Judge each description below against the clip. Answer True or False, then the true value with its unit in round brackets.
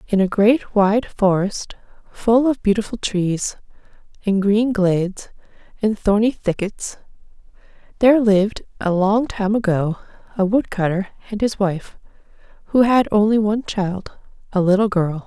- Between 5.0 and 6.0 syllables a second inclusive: False (4.5 syllables/s)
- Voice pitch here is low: False (205 Hz)